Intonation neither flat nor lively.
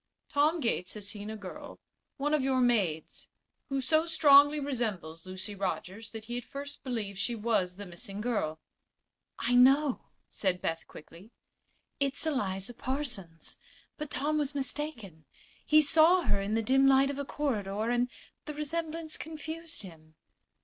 No: wide, 6.6 semitones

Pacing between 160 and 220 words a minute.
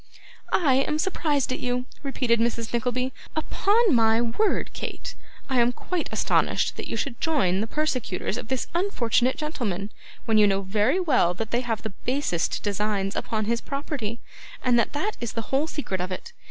Yes: average, 180 wpm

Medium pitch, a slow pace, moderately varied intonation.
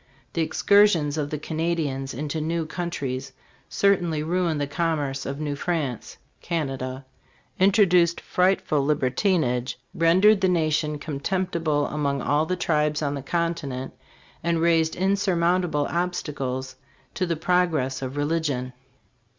Yes: medium, 155 Hz; slow, 125 wpm; average, 3.5 semitones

